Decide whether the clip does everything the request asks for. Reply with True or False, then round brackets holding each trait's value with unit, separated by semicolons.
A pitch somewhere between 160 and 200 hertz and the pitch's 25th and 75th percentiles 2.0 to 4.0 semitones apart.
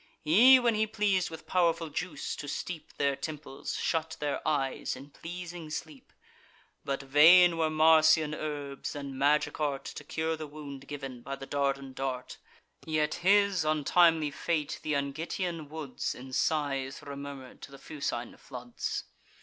False (150 Hz; 2.8 semitones)